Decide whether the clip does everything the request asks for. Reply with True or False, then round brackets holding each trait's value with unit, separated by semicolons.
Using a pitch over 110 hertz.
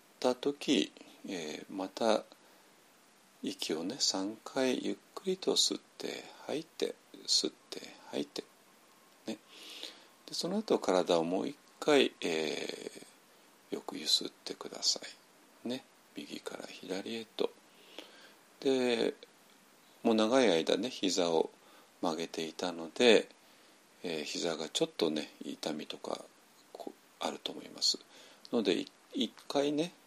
True (135 Hz)